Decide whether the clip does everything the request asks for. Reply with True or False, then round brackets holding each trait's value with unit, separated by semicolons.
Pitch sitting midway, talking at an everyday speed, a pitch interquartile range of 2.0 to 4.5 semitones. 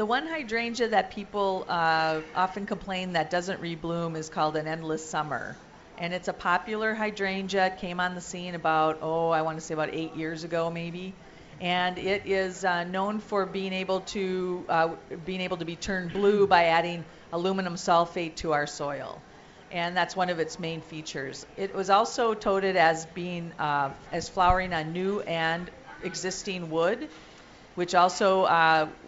True (180 Hz; 175 wpm; 2.8 semitones)